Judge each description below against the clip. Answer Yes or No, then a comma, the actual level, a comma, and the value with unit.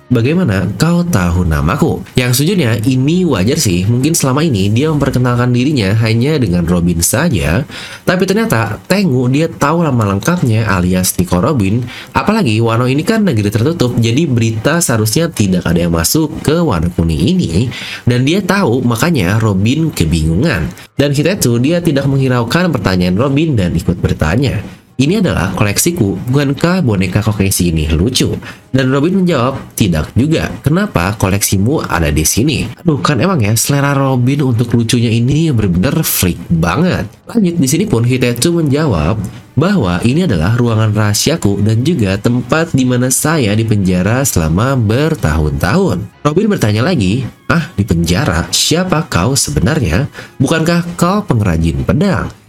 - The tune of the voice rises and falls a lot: Yes, wide, 7.8 semitones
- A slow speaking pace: No, average, 145 wpm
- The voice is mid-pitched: No, low, 120 Hz